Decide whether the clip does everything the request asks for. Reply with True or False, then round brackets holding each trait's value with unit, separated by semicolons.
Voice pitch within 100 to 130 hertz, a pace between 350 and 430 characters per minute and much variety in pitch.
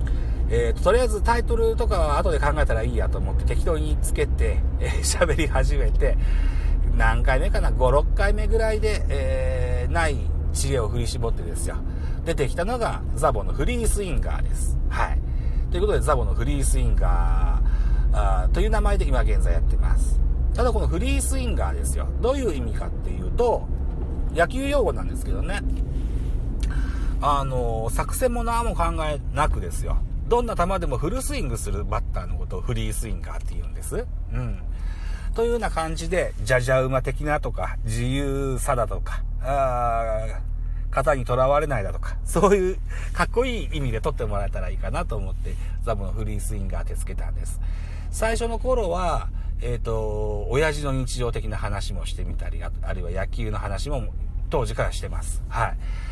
False (80 Hz; 360 characters per minute; 8.5 semitones)